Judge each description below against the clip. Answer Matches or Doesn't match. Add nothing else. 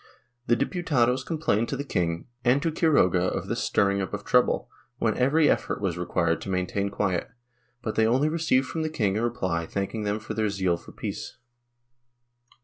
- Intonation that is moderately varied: Doesn't match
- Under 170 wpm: Doesn't match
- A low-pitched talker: Matches